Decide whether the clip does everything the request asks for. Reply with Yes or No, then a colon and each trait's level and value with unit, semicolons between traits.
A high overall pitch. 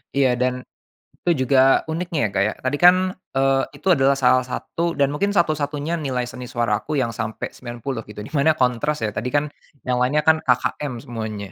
No: low, 135 Hz